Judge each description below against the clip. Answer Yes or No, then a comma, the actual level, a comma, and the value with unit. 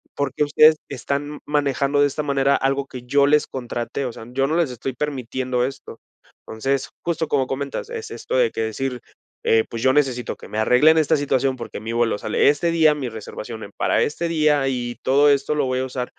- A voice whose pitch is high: No, low, 135 Hz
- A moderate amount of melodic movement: Yes, average, 3.0 semitones